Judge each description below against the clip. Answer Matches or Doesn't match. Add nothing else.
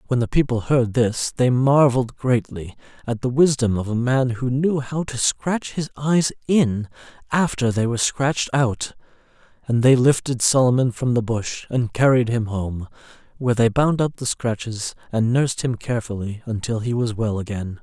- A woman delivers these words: Doesn't match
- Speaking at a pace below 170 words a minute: Doesn't match